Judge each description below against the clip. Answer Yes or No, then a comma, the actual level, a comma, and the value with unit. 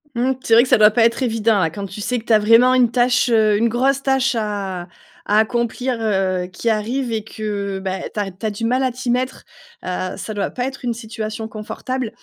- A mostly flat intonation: No, average, 3.0 semitones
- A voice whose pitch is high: Yes, high, 225 Hz